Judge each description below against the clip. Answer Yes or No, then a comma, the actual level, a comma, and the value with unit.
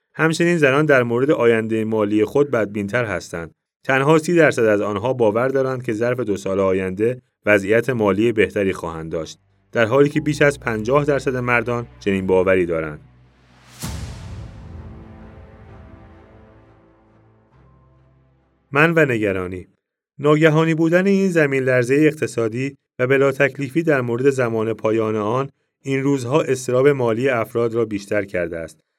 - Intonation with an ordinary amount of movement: No, wide, 5.7 semitones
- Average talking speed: Yes, average, 130 wpm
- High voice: No, low, 110 Hz